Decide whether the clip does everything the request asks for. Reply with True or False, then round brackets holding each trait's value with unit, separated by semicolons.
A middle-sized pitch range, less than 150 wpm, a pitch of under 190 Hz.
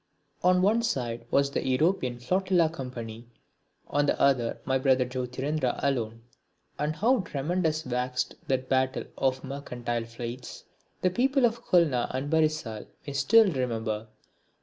True (4.4 semitones; 140 wpm; 135 Hz)